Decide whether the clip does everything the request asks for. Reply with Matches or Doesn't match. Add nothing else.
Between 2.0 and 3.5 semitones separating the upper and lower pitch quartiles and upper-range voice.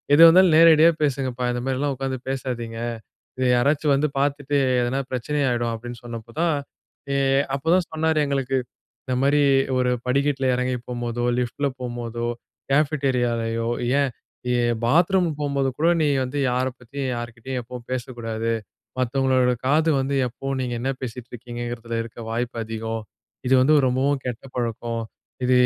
Doesn't match